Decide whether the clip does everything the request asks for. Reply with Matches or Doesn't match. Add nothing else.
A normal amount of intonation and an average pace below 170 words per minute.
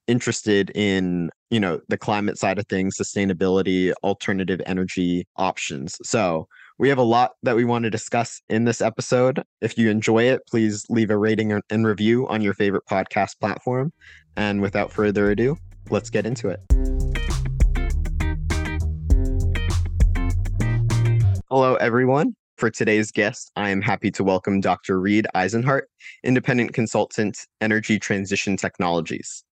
Matches